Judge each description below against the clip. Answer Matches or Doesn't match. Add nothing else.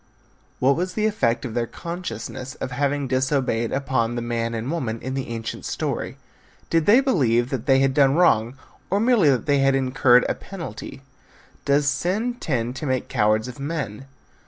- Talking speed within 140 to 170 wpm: Doesn't match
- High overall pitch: Doesn't match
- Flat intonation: Doesn't match